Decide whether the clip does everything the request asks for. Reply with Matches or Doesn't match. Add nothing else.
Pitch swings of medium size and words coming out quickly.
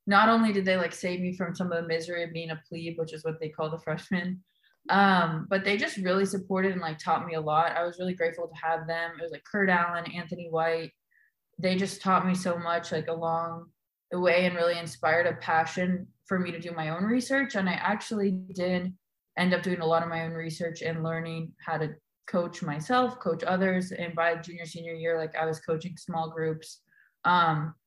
Doesn't match